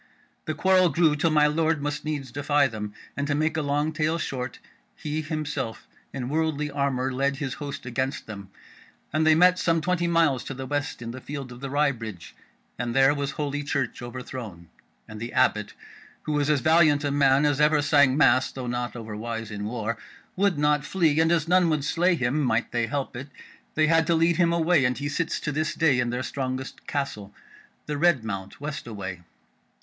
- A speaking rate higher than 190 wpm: Yes, fast, 205 wpm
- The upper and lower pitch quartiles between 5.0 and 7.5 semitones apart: No, average, 3.7 semitones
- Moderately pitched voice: Yes, medium, 145 Hz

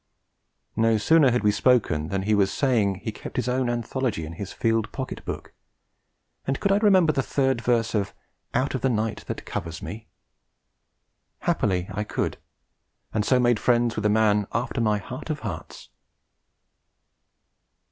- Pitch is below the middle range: Yes, low, 115 Hz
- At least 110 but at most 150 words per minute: No, average, 165 wpm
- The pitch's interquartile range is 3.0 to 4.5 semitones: Yes, average, 3.4 semitones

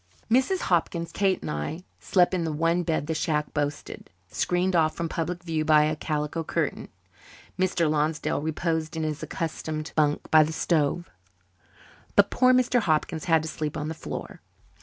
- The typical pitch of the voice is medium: Yes, medium, 160 Hz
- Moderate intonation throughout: No, narrow, 2.2 semitones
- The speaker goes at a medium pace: Yes, average, 170 wpm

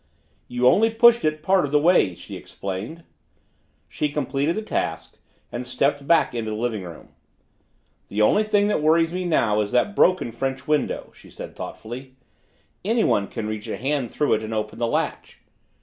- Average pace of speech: Yes, average, 180 wpm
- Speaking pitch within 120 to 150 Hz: Yes, low, 135 Hz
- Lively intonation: Yes, wide, 7.2 semitones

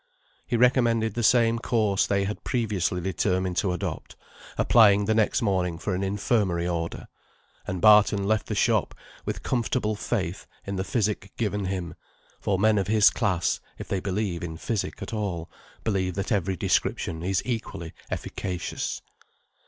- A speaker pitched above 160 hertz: No, low, 100 Hz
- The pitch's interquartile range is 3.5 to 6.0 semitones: No, average, 3.0 semitones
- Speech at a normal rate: Yes, average, 155 wpm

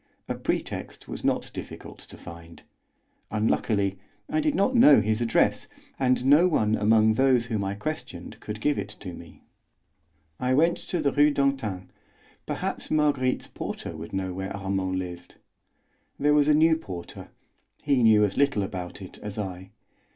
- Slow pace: No, average, 160 wpm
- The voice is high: No, low, 110 Hz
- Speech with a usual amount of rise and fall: No, wide, 6.8 semitones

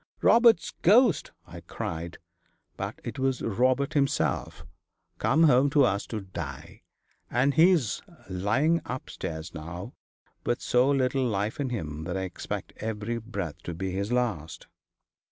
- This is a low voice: Yes, low, 120 Hz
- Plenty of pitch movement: Yes, wide, 6.5 semitones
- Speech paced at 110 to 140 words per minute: Yes, slow, 135 wpm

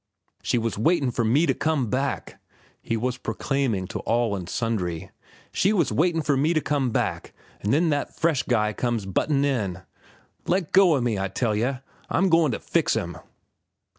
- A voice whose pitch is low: Yes, low, 130 Hz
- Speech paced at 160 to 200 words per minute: Yes, average, 185 wpm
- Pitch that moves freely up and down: Yes, wide, 5.7 semitones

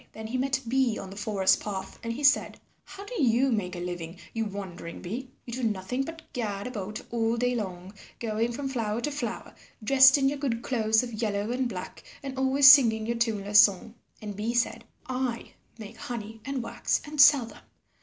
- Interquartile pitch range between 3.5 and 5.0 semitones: Yes, average, 3.9 semitones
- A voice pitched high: Yes, high, 230 Hz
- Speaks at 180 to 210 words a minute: Yes, average, 200 wpm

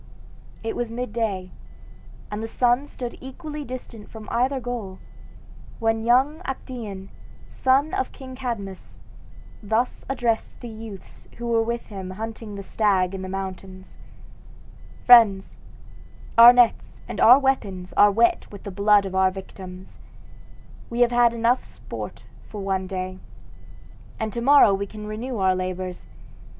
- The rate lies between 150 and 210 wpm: No, average, 140 wpm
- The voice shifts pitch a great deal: No, average, 4.0 semitones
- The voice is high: Yes, high, 220 Hz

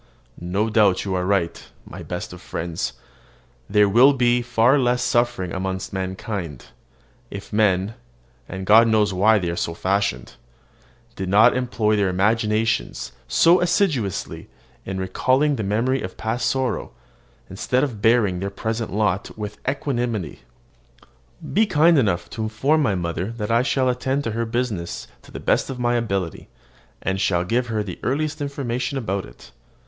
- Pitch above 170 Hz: No, low, 110 Hz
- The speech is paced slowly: No, average, 155 wpm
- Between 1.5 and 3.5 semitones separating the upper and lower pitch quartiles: No, average, 4.6 semitones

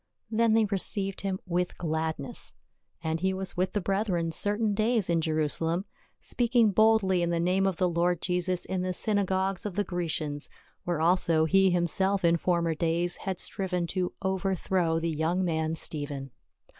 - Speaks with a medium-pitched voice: Yes, medium, 180 Hz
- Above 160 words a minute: Yes, average, 170 wpm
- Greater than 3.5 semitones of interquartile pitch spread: No, narrow, 2.6 semitones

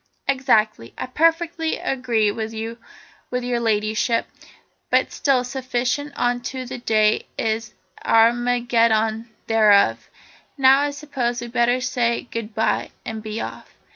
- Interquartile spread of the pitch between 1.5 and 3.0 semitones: Yes, narrow, 2.5 semitones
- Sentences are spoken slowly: Yes, slow, 115 wpm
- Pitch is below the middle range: No, high, 240 Hz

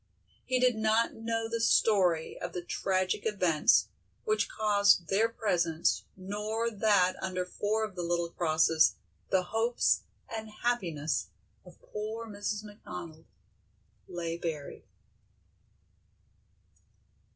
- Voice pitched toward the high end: Yes, high, 200 Hz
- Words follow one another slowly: Yes, slow, 110 wpm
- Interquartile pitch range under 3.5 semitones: No, average, 4.2 semitones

